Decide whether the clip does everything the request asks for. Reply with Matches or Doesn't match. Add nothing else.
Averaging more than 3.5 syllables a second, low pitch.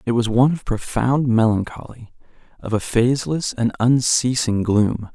Matches